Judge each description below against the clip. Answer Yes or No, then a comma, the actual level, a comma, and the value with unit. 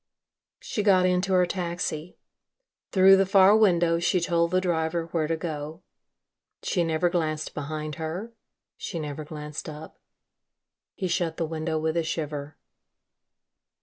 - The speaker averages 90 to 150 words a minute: Yes, average, 140 wpm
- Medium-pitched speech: Yes, medium, 165 Hz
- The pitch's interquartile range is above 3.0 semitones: No, narrow, 2.6 semitones